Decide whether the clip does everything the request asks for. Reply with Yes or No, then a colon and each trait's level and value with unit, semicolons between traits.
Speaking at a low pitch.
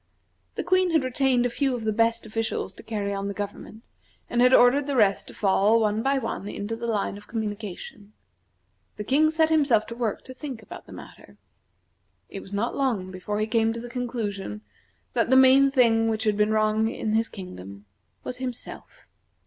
No: high, 225 Hz